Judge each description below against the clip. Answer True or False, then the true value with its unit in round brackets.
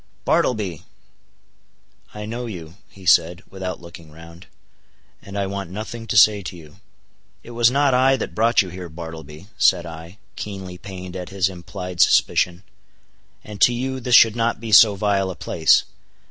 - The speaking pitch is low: True (95 Hz)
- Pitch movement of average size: True (4.0 semitones)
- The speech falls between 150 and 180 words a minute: True (160 wpm)